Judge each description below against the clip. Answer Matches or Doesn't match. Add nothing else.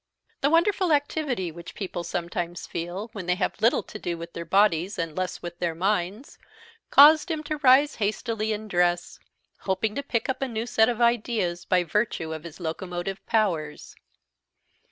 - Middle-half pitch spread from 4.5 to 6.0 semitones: Matches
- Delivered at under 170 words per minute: Doesn't match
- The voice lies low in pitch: Doesn't match